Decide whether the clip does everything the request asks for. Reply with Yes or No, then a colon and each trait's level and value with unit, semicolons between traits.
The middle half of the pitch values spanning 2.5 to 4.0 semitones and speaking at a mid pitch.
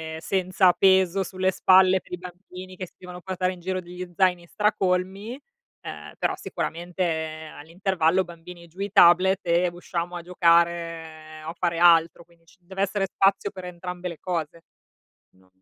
No: narrow, 1.8 semitones; medium, 180 Hz